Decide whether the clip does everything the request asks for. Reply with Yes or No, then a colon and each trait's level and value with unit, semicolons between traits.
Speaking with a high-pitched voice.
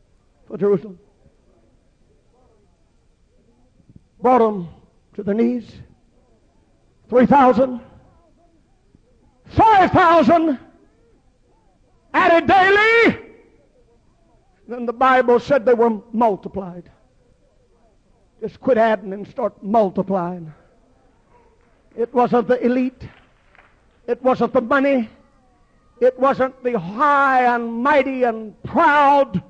Yes: high, 245 Hz